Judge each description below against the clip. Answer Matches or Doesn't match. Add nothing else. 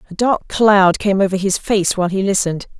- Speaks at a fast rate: Matches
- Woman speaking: Matches